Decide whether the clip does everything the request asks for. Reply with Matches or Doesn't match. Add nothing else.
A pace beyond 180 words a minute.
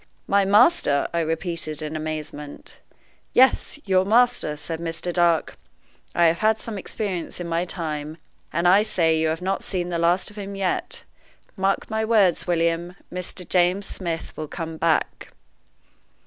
Doesn't match